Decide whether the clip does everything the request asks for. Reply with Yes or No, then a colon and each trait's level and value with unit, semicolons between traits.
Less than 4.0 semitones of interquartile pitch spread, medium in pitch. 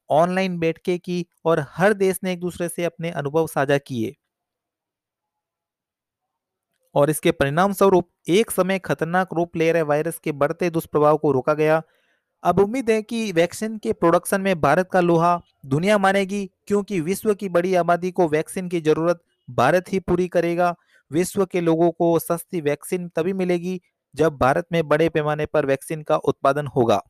Yes: average, 3.1 semitones; medium, 170 Hz